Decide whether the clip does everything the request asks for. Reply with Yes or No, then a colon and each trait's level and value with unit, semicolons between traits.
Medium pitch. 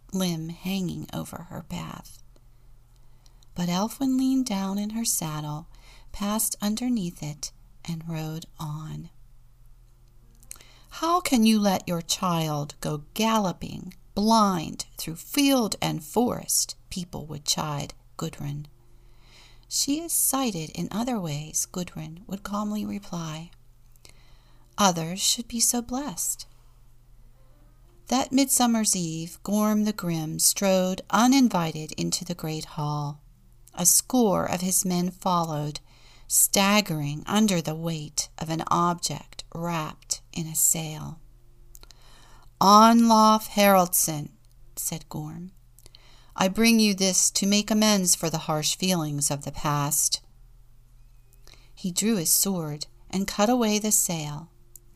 Yes: medium, 160 Hz